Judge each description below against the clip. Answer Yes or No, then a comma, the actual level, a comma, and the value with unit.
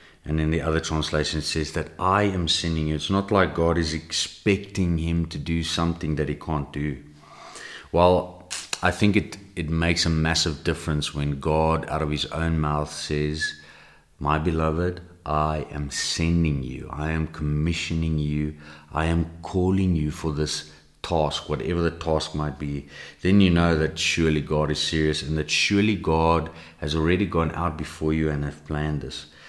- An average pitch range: No, narrow, 1.7 semitones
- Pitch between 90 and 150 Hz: No, very low, 80 Hz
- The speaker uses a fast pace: No, average, 175 wpm